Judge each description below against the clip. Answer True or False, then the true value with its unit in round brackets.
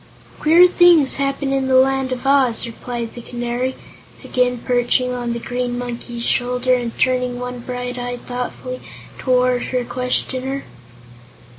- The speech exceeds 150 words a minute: False (140 wpm)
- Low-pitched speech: False (250 Hz)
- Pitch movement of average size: False (1.2 semitones)